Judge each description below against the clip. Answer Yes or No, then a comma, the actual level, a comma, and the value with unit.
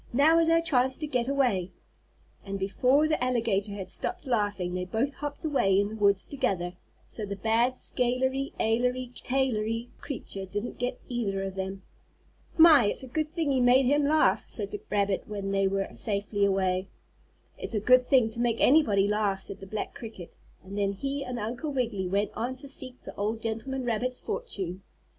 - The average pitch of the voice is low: No, high, 230 Hz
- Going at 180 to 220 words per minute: Yes, average, 190 wpm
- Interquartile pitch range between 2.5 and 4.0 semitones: No, average, 4.8 semitones